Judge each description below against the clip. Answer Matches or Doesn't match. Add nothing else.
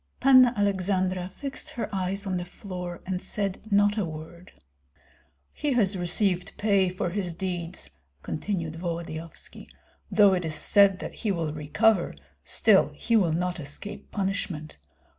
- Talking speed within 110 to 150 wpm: Matches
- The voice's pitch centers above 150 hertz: Matches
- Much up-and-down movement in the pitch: Doesn't match